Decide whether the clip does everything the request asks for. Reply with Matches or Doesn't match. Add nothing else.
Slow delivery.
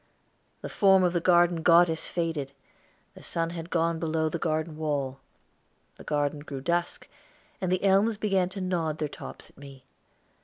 Doesn't match